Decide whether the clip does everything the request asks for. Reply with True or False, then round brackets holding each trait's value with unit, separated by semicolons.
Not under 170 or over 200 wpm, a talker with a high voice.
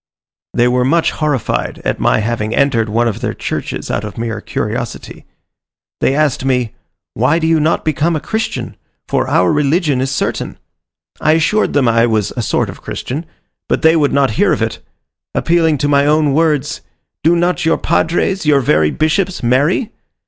False (180 wpm; 145 Hz)